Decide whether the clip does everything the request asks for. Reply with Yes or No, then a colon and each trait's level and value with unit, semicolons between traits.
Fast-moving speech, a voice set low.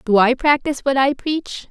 No: fast, 210 wpm; very high, 270 Hz